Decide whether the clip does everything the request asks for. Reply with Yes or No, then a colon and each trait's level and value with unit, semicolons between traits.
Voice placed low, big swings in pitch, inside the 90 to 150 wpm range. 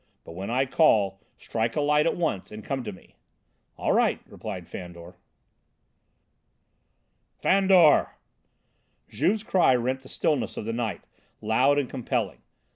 Yes: low, 125 Hz; wide, 6.4 semitones; slow, 135 wpm